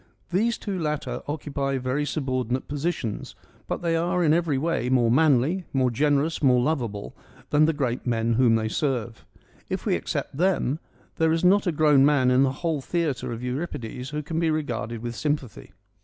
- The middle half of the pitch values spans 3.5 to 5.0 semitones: Yes, average, 4.3 semitones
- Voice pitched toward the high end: No, medium, 140 Hz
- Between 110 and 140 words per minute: No, average, 180 wpm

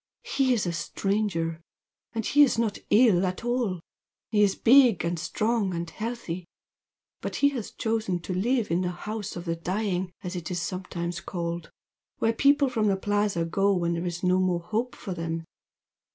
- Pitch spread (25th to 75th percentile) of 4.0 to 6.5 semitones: Yes, average, 4.4 semitones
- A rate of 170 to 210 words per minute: Yes, average, 175 wpm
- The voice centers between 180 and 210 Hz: Yes, high, 190 Hz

